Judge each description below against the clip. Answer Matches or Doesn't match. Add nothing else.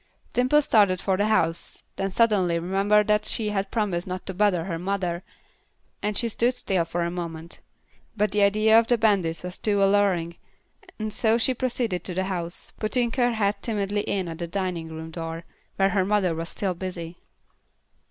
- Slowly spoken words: Doesn't match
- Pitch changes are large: Doesn't match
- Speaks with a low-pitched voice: Doesn't match